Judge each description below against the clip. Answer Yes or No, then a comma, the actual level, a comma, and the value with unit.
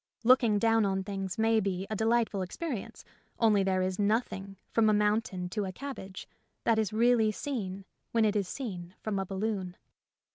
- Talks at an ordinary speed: Yes, average, 175 wpm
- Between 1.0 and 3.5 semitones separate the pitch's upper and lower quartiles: Yes, average, 2.8 semitones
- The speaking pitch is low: No, high, 210 Hz